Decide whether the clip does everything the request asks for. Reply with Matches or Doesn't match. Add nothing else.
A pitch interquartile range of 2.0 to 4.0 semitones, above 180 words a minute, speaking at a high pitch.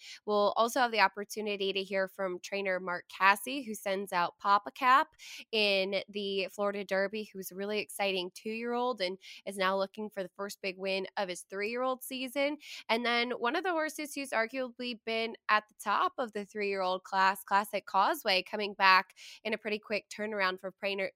Matches